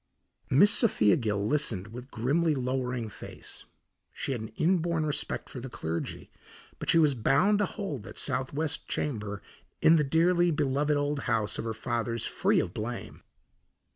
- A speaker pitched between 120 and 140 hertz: Yes, low, 135 Hz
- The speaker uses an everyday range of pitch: No, wide, 5.7 semitones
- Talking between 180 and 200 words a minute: No, average, 160 wpm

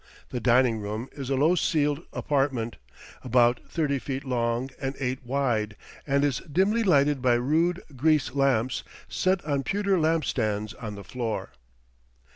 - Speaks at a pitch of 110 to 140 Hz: Yes, low, 135 Hz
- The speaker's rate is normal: Yes, average, 150 wpm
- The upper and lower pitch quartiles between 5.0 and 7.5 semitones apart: No, average, 3.8 semitones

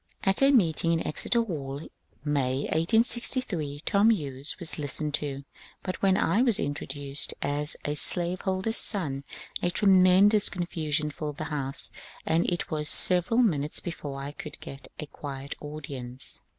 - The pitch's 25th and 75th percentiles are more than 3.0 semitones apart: Yes, average, 4.7 semitones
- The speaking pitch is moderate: Yes, medium, 155 Hz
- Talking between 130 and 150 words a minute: Yes, average, 145 wpm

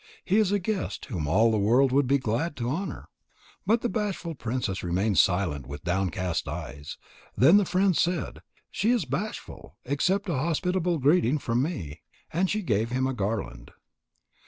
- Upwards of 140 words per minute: Yes, average, 170 wpm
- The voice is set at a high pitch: No, low, 135 Hz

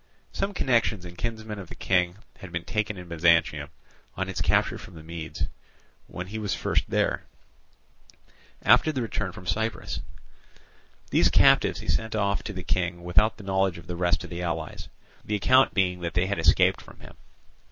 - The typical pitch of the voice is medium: No, very low, 90 Hz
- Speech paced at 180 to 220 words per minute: Yes, average, 185 wpm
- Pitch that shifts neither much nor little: Yes, average, 3.6 semitones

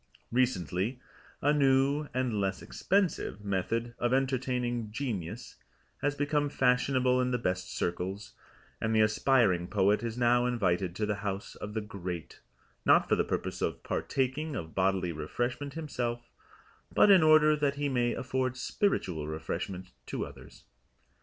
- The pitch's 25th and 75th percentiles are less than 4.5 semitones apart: No, wide, 5.5 semitones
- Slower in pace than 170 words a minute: Yes, average, 145 wpm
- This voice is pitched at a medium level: No, low, 120 Hz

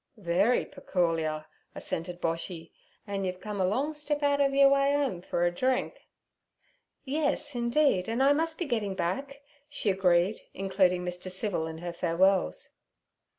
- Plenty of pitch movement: Yes, wide, 7.7 semitones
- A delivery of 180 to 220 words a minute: No, average, 150 wpm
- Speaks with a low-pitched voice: No, high, 195 Hz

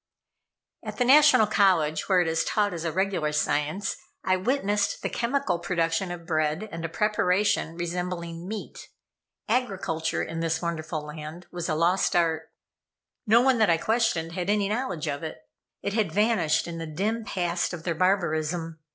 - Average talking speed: Yes, average, 170 wpm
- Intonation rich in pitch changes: No, average, 4.1 semitones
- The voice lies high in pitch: No, medium, 175 Hz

